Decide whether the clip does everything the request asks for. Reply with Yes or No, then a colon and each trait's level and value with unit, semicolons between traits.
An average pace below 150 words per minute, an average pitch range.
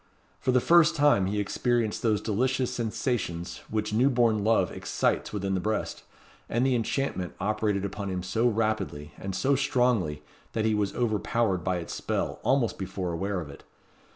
No: average, 170 wpm; average, 4.1 semitones